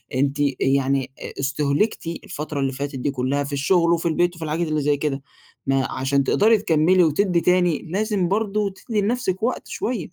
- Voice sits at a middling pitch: Yes, medium, 160 Hz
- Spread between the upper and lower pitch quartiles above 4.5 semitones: Yes, average, 5.2 semitones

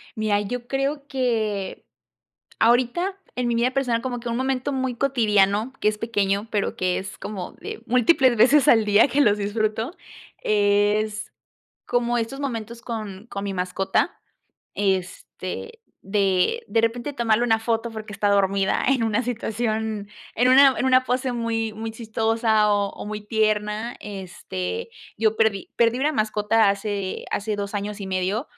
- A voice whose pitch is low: No, high, 220 Hz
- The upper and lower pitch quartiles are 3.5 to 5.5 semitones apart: No, average, 2.9 semitones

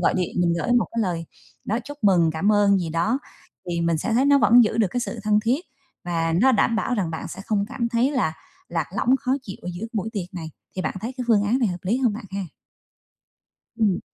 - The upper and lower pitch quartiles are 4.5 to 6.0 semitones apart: Yes, average, 5.1 semitones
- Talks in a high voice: Yes, high, 210 Hz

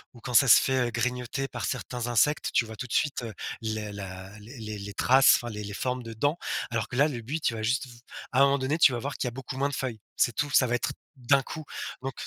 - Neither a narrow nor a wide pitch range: Yes, average, 3.3 semitones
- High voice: No, low, 125 Hz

